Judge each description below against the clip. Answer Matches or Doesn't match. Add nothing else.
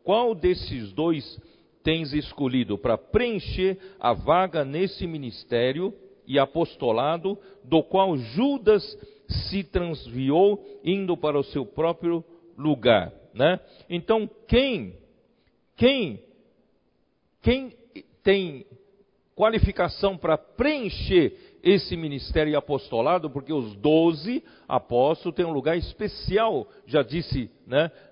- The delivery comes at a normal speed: Doesn't match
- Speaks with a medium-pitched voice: Matches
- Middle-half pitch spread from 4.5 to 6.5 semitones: Matches